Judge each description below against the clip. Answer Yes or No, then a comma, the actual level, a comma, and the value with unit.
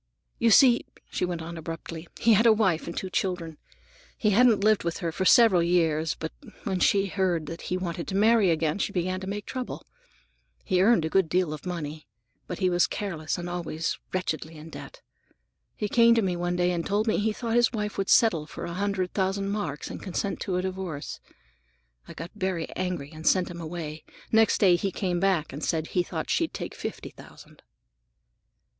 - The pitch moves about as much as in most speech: Yes, average, 3.3 semitones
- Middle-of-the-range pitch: Yes, medium, 180 Hz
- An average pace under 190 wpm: No, fast, 205 wpm